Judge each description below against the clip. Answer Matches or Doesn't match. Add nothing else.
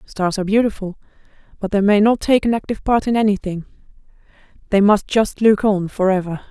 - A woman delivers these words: Matches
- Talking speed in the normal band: Matches